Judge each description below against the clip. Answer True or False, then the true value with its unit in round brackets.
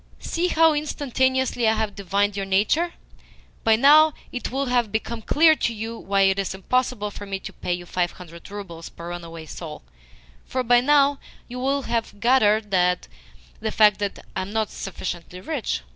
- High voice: True (215 Hz)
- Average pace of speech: True (175 wpm)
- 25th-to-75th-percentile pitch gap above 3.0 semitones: True (5.2 semitones)